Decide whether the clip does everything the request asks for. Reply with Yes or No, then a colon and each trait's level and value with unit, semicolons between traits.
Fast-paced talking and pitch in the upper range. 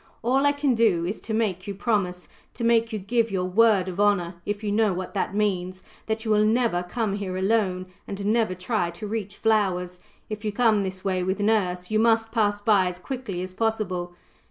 Yes: fast, 210 wpm; high, 205 Hz